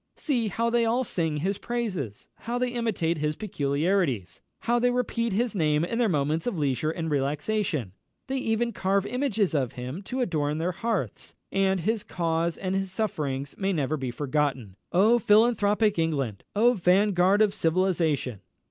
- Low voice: No, medium, 185 Hz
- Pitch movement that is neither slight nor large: No, wide, 6.8 semitones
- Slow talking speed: No, average, 165 wpm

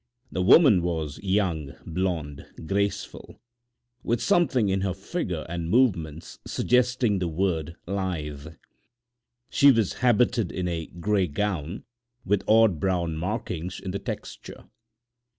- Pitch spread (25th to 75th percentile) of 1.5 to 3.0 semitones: No, average, 4.2 semitones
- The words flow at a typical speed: No, slow, 120 wpm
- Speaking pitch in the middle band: No, very low, 95 Hz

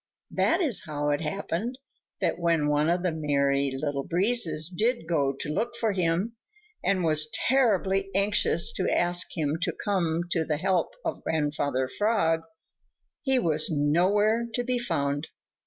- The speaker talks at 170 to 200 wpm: No, average, 155 wpm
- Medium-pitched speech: Yes, medium, 170 Hz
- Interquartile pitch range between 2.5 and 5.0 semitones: No, wide, 5.4 semitones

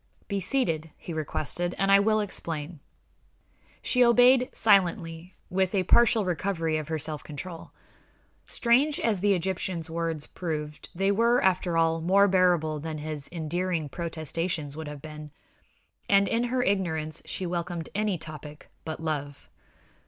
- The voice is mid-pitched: Yes, medium, 175 Hz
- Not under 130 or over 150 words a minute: Yes, average, 145 wpm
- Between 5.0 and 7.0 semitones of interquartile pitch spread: No, average, 3.9 semitones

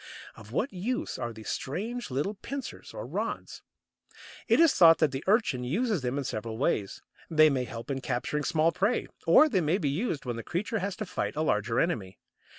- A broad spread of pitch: Yes, wide, 8.2 semitones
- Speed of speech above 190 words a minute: Yes, average, 200 wpm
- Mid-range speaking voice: Yes, medium, 155 Hz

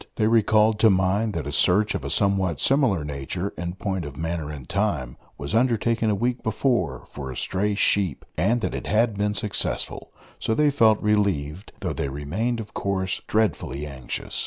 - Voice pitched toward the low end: Yes, low, 100 Hz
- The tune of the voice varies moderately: No, wide, 5.8 semitones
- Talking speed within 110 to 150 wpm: No, average, 185 wpm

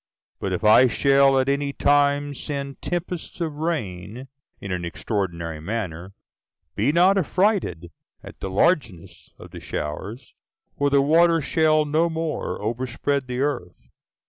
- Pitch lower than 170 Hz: Yes, low, 135 Hz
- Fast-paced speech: No, average, 140 wpm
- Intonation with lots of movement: Yes, wide, 7.5 semitones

